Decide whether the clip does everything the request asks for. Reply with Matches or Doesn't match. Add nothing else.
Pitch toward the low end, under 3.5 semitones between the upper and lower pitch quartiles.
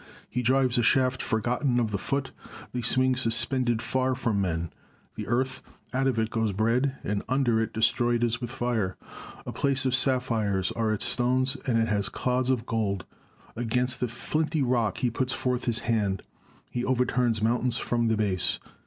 Matches